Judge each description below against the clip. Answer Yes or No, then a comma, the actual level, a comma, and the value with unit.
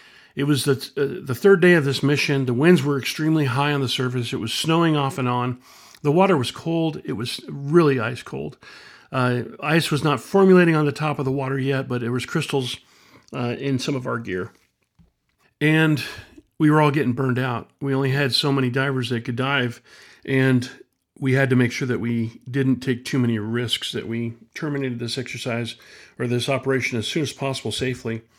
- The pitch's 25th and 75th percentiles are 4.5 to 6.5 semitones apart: No, average, 2.9 semitones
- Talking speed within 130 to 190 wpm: No, fast, 205 wpm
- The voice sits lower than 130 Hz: No, low, 135 Hz